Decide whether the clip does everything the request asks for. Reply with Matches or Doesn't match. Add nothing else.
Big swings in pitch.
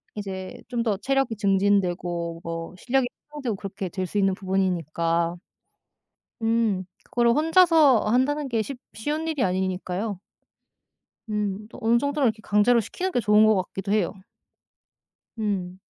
Doesn't match